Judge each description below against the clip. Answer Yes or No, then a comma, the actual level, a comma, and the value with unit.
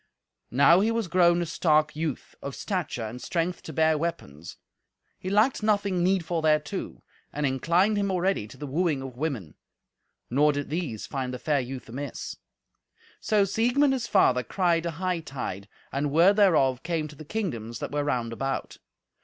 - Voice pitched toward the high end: No, medium, 160 Hz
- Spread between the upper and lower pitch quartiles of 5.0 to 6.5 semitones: Yes, wide, 5.5 semitones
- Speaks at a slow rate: No, average, 170 wpm